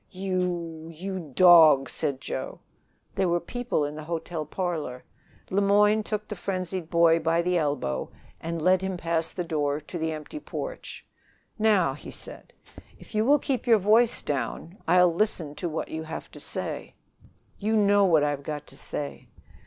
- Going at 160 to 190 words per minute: Yes, average, 170 wpm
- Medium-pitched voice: Yes, medium, 170 Hz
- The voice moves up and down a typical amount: Yes, average, 3.9 semitones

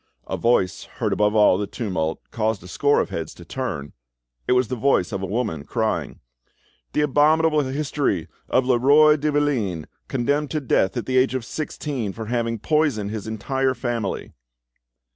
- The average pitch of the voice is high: No, low, 120 Hz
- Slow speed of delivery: No, average, 170 wpm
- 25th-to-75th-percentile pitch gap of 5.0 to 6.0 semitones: Yes, wide, 5.4 semitones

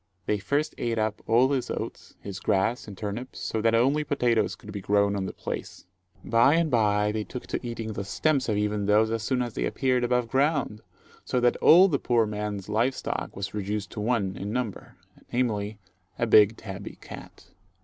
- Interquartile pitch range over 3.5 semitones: No, average, 3.2 semitones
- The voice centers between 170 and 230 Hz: No, low, 110 Hz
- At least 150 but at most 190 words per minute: No, average, 200 wpm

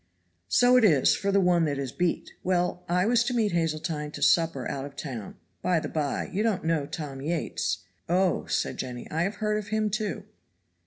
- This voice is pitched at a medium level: Yes, medium, 170 Hz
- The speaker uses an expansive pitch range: Yes, wide, 5.7 semitones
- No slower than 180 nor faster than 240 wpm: Yes, fast, 205 wpm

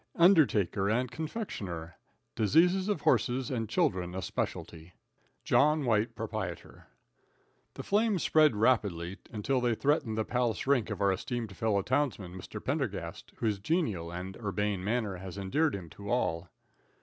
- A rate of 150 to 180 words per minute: No, average, 140 wpm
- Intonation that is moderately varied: No, wide, 6.2 semitones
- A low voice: Yes, low, 110 Hz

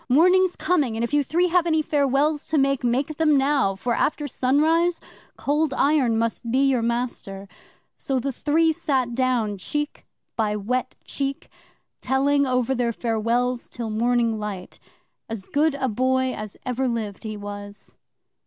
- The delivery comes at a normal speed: Yes, average, 155 wpm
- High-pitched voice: Yes, very high, 255 Hz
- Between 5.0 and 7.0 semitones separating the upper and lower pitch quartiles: No, average, 4.0 semitones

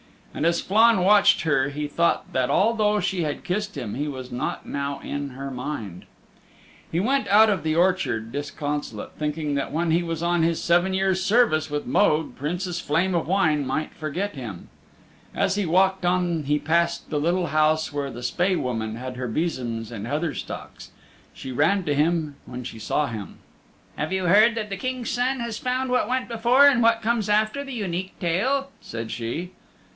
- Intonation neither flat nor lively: No, wide, 5.7 semitones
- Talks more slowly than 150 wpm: No, average, 190 wpm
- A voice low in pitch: No, medium, 170 Hz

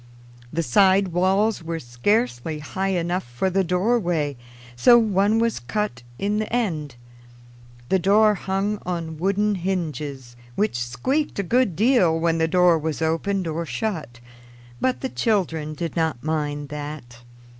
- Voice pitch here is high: No, medium, 175 Hz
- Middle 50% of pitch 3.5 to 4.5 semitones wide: No, average, 4.9 semitones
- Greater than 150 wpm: No, average, 145 wpm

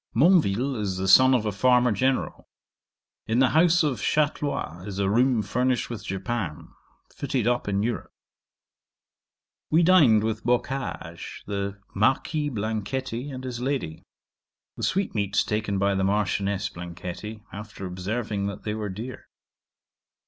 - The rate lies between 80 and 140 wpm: Yes, slow, 135 wpm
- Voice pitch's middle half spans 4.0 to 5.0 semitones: Yes, average, 4.6 semitones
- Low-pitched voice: Yes, low, 110 Hz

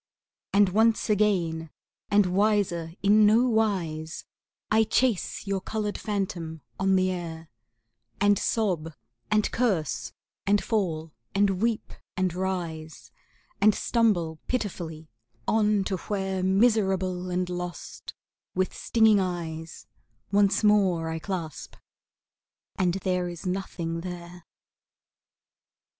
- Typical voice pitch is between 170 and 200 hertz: Yes, medium, 185 Hz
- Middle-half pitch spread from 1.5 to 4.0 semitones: Yes, average, 3.5 semitones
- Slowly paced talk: Yes, slow, 110 wpm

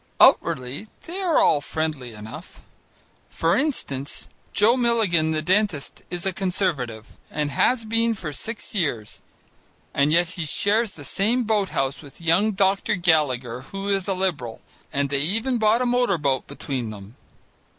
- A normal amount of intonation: No, wide, 7.2 semitones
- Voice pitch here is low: No, medium, 175 Hz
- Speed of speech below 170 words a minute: Yes, average, 155 wpm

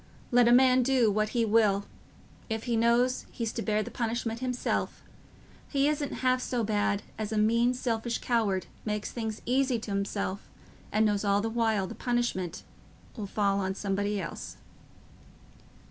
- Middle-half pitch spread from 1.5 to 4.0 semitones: Yes, average, 2.8 semitones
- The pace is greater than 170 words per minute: No, average, 165 wpm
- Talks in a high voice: Yes, high, 225 Hz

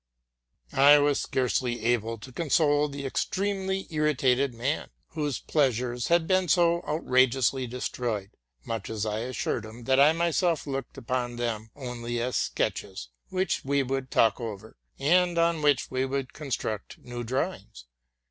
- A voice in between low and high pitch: No, low, 130 Hz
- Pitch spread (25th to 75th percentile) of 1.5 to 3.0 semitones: No, average, 4.2 semitones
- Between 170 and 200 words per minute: No, average, 145 wpm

